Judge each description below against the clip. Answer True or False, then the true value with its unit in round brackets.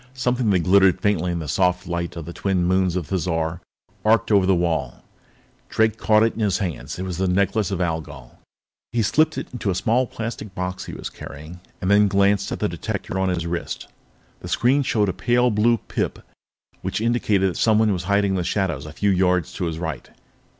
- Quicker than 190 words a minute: True (205 wpm)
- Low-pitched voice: True (95 Hz)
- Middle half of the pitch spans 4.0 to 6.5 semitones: False (3.6 semitones)